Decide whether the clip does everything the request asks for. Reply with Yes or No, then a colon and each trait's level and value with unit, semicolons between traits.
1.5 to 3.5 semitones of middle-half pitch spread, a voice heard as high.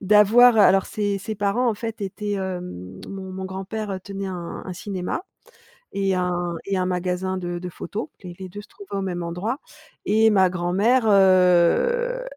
Yes: narrow, 2.5 semitones; high, 195 Hz